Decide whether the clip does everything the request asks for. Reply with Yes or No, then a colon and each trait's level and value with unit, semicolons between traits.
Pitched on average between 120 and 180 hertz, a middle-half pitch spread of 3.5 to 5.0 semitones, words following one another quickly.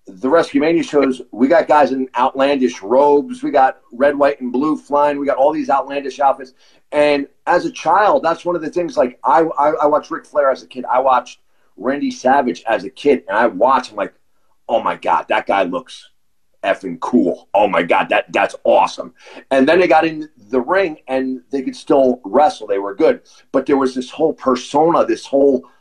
No: medium, 140 Hz; average, 2.8 semitones; fast, 210 wpm